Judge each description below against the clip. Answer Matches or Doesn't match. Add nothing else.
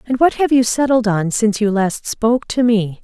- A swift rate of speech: Matches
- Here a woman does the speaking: Matches